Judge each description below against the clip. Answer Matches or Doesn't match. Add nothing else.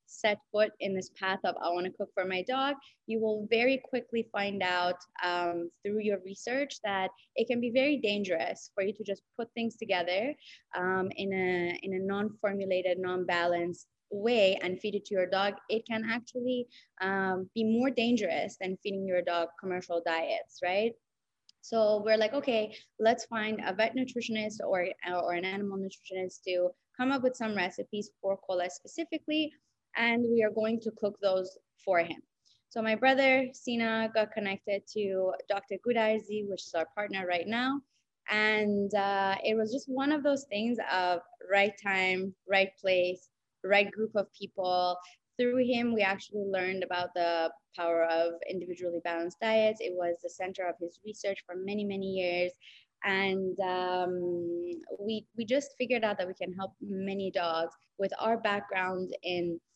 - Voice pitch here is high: Matches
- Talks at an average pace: Matches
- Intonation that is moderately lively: Matches